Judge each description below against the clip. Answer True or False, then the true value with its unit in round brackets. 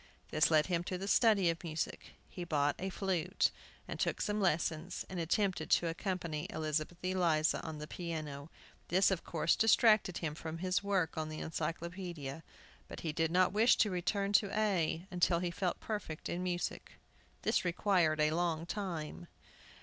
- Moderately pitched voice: True (175 Hz)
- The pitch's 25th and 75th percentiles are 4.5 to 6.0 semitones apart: False (3.0 semitones)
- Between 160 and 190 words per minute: True (170 wpm)